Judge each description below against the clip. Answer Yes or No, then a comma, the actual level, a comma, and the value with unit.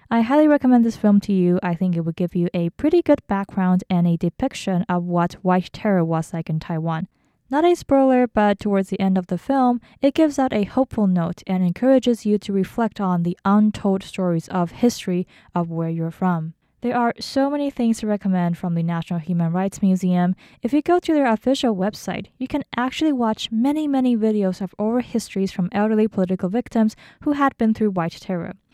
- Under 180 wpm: No, fast, 205 wpm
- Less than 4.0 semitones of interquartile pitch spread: No, average, 5.3 semitones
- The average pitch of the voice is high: Yes, high, 200 Hz